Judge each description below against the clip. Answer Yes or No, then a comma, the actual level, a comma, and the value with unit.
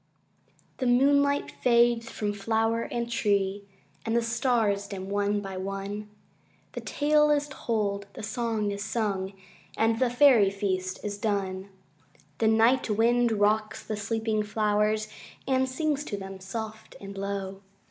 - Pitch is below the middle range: No, high, 215 Hz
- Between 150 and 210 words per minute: No, average, 140 wpm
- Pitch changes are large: No, average, 2.8 semitones